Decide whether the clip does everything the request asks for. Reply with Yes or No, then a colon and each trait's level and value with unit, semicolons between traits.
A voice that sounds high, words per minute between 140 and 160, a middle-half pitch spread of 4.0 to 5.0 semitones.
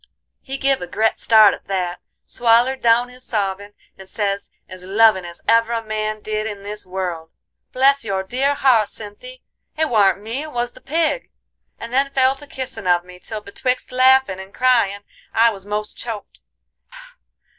No: high, 220 Hz; average, 175 wpm; average, 4.4 semitones